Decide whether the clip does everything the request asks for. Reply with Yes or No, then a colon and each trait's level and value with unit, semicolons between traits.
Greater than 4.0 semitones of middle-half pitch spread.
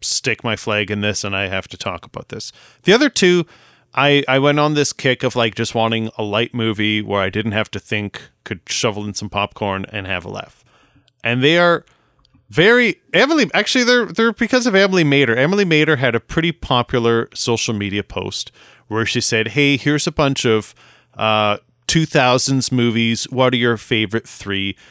Yes: wide, 5.4 semitones